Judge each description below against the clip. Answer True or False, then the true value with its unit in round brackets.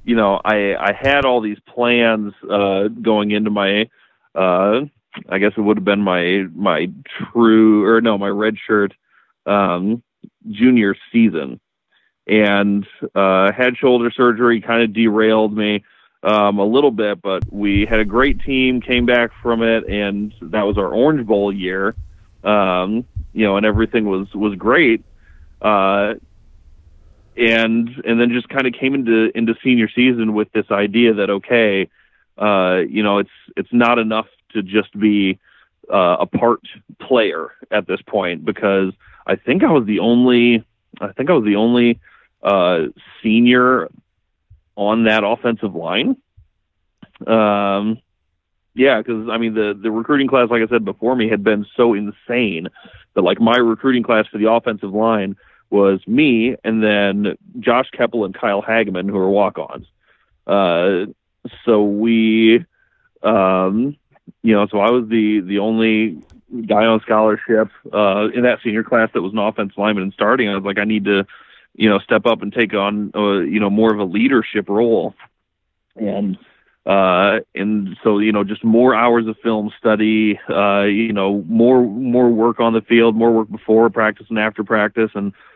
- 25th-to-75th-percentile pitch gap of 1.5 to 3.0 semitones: True (2.4 semitones)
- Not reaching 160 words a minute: False (165 wpm)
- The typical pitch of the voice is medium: False (110 Hz)